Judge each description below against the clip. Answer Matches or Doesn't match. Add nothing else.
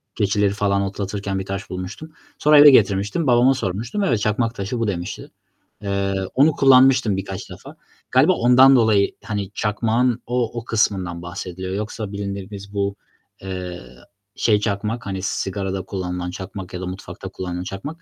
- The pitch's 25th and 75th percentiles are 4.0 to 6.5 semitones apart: Doesn't match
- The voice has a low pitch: Matches